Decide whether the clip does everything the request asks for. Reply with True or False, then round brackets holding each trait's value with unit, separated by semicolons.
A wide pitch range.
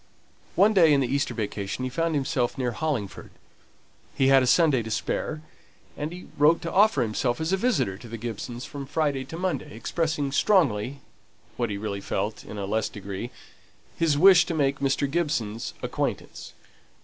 True (5.7 semitones)